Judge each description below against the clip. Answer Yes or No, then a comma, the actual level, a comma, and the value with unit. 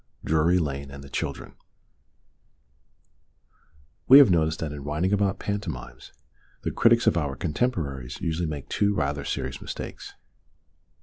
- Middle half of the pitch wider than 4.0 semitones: Yes, wide, 5.6 semitones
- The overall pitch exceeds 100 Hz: No, very low, 80 Hz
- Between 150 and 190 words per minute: No, slow, 135 wpm